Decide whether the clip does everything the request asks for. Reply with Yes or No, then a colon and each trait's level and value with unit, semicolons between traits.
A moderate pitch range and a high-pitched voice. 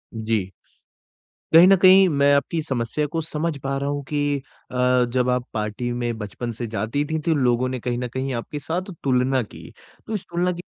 No: average, 4.1 semitones; low, 135 Hz